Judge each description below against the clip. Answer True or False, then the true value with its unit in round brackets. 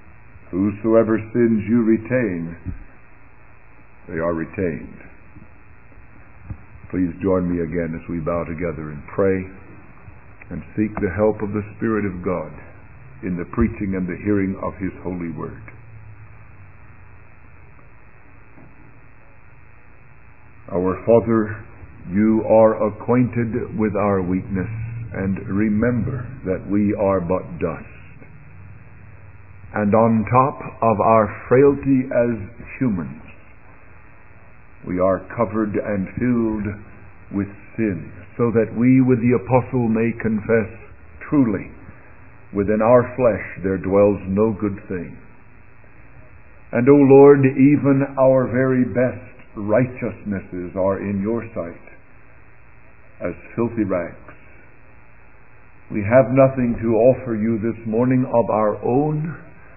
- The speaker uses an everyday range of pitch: True (3.6 semitones)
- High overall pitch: False (110 Hz)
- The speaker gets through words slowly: True (110 wpm)